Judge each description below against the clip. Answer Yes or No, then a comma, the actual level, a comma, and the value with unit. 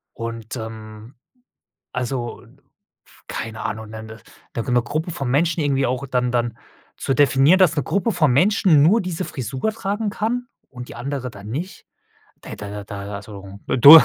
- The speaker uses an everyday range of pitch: No, wide, 6.4 semitones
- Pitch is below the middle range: Yes, low, 130 Hz